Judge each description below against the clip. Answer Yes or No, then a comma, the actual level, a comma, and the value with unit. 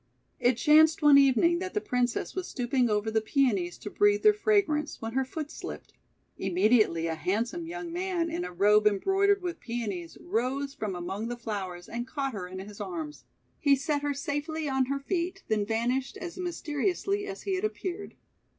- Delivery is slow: No, average, 185 wpm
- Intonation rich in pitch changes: Yes, wide, 7.9 semitones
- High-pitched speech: Yes, very high, 275 Hz